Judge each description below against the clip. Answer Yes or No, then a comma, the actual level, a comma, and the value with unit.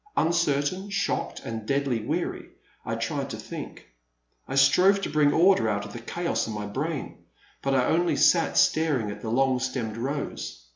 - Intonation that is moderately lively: No, wide, 6.2 semitones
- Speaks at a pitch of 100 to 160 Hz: Yes, low, 135 Hz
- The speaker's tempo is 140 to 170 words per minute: No, average, 180 wpm